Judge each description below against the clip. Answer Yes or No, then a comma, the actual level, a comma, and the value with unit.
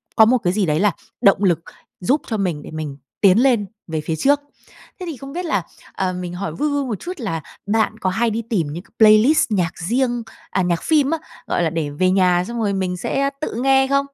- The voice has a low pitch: No, high, 205 Hz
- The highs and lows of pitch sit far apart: Yes, wide, 6.2 semitones